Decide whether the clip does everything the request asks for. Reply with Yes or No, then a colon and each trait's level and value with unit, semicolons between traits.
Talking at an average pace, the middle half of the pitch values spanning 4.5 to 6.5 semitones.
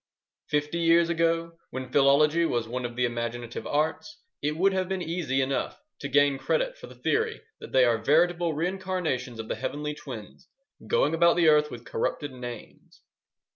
Yes: average, 175 wpm; average, 5.0 semitones